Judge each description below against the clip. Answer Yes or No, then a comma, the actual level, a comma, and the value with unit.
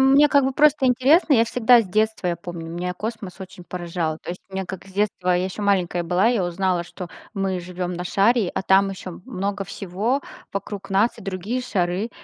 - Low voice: No, high, 195 Hz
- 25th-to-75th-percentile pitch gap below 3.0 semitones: No, average, 4.1 semitones